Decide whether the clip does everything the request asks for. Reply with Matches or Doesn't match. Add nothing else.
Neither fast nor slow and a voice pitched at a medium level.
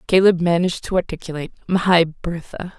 Doesn't match